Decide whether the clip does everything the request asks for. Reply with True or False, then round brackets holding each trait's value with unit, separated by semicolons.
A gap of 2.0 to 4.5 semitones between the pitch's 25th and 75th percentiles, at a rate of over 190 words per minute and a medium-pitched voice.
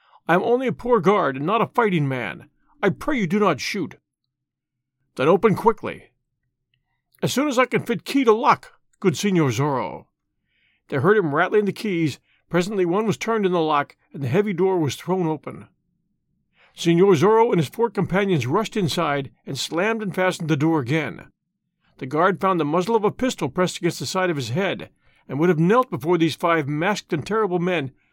False (5.6 semitones; 200 wpm; 175 Hz)